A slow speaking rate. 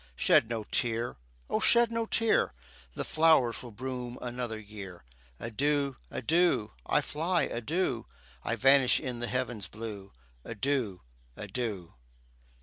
Yes: slow, 125 wpm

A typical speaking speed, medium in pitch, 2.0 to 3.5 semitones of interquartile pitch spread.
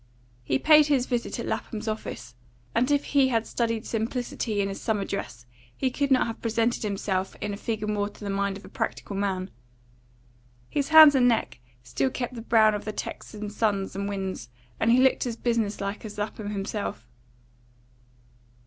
No: average, 185 wpm; high, 215 Hz; average, 3.1 semitones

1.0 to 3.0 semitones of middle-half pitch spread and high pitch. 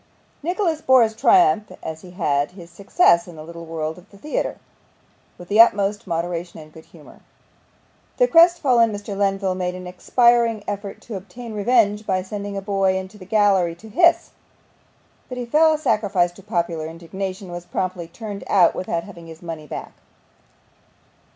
No: average, 4.1 semitones; high, 195 Hz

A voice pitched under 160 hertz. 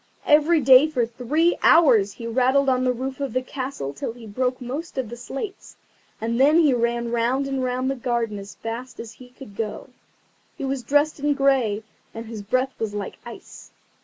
No: very high, 255 Hz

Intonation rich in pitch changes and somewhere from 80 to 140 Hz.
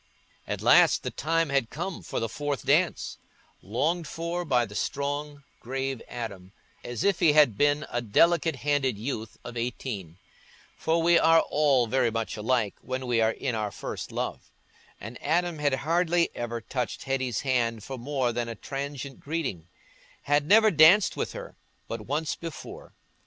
No: average, 5.0 semitones; low, 135 Hz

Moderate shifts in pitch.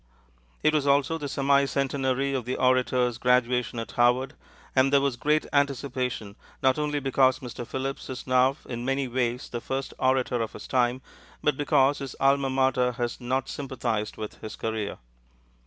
No: narrow, 2.0 semitones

